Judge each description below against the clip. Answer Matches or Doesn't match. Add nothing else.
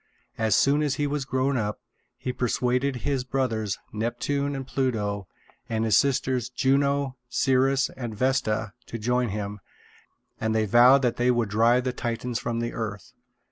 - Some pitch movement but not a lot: Matches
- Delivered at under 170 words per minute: Matches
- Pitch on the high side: Doesn't match